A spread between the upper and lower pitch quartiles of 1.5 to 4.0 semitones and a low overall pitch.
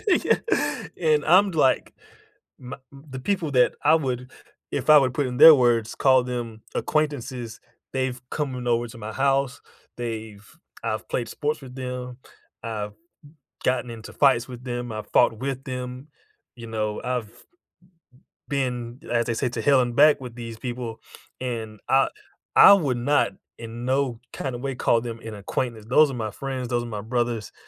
Yes: narrow, 2.6 semitones; low, 125 Hz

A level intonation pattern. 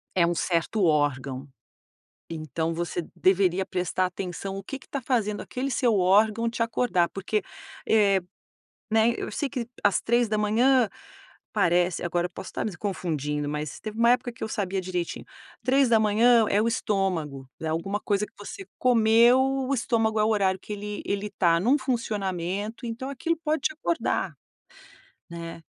No: average, 4.8 semitones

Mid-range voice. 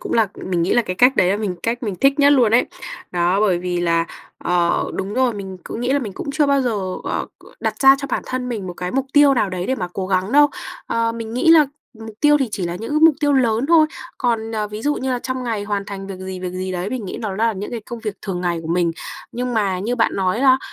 No: high, 220 Hz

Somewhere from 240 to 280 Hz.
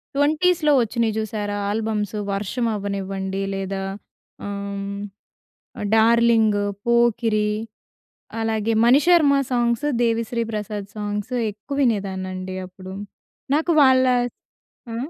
No: high, 220 Hz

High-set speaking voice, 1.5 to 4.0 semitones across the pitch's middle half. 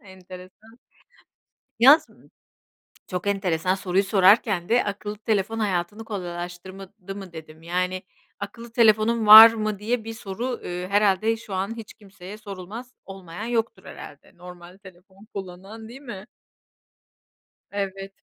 Yes: high, 195 Hz; average, 3.2 semitones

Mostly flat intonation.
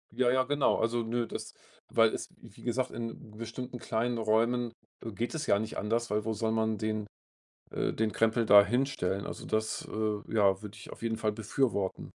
Yes: narrow, 1.8 semitones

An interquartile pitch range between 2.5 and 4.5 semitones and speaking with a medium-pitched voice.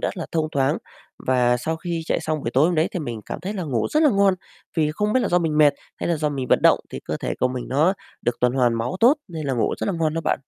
No: average, 5.1 semitones; medium, 155 Hz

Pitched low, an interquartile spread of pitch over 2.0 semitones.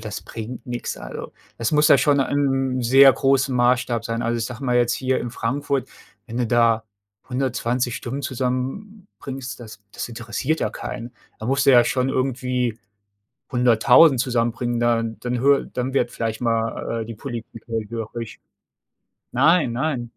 Yes: low, 125 Hz; narrow, 2.4 semitones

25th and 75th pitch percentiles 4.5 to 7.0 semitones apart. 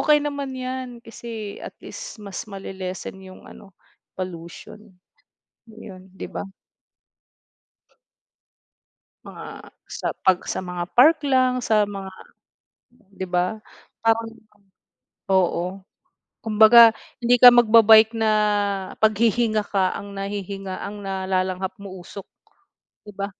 No: average, 3.3 semitones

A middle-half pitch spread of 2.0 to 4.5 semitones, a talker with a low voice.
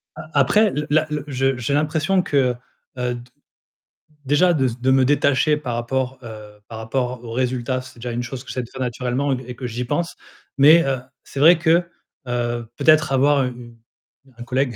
Yes: average, 3.2 semitones; low, 130 Hz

